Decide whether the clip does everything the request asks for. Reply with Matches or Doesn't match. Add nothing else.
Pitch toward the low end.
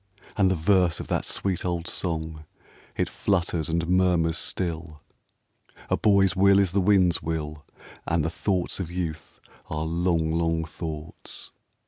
Matches